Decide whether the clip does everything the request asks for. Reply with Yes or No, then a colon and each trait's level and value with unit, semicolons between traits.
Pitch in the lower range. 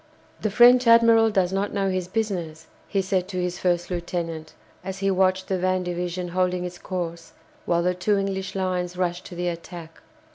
No: medium, 185 Hz